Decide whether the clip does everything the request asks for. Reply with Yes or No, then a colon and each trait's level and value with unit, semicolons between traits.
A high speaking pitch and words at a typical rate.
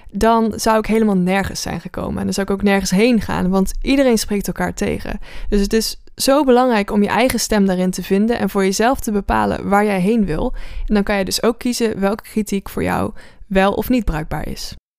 No: high, 205 Hz; fast, 230 wpm